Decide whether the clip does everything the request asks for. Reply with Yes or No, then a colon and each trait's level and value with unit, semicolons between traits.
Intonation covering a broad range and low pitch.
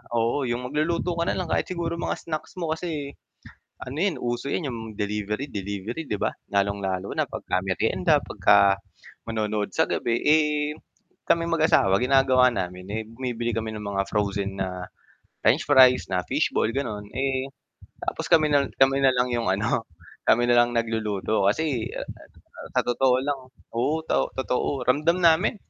Yes: wide, 5.9 semitones; low, 125 Hz